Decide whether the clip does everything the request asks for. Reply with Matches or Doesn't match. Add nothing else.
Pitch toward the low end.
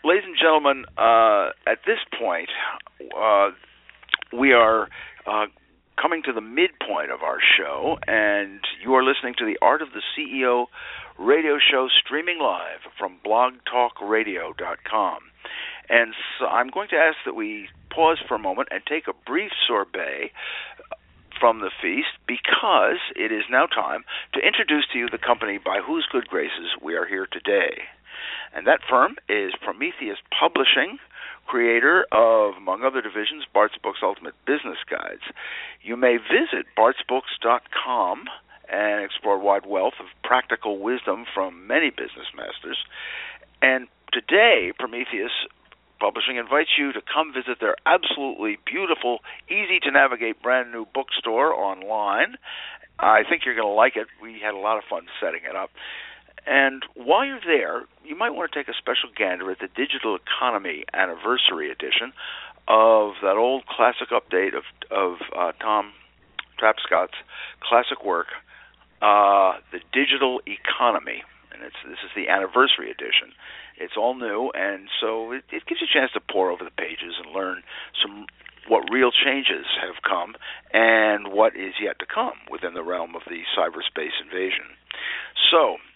Matches